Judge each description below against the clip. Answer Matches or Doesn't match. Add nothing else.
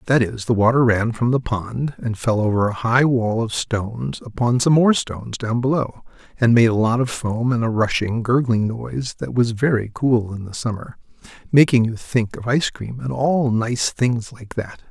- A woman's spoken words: Doesn't match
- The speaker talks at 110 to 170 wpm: Doesn't match